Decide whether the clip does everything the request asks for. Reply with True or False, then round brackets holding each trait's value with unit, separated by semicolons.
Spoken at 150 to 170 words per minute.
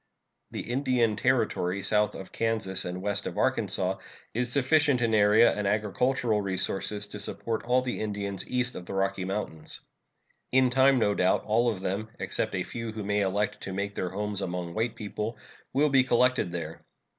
False (180 wpm)